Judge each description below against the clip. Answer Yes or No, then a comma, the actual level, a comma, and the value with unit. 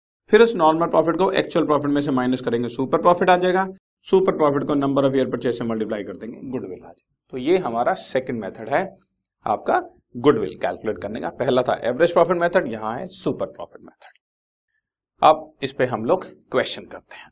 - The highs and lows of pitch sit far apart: Yes, wide, 5.7 semitones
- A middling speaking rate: No, fast, 200 wpm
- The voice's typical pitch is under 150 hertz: No, medium, 155 Hz